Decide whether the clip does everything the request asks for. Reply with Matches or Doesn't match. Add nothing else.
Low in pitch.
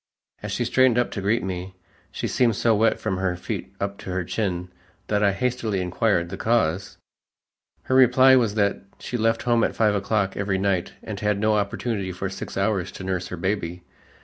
Matches